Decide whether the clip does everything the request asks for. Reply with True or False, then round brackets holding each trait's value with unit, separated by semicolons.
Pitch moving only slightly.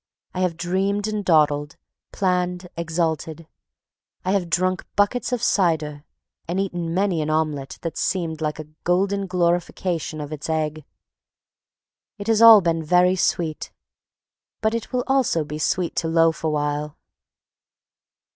False (3.4 semitones)